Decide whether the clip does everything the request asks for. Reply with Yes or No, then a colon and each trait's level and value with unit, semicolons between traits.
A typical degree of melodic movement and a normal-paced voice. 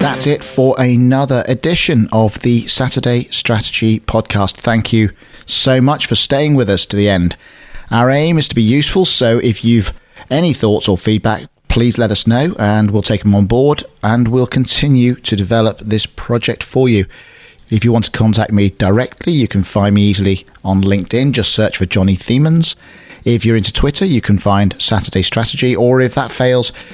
Yes: average, 3.7 semitones; average, 190 wpm